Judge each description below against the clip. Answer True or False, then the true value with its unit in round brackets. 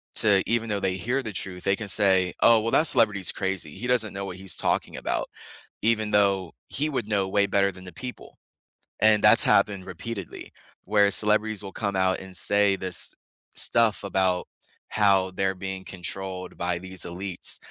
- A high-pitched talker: False (100 Hz)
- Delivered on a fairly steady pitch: True (2.2 semitones)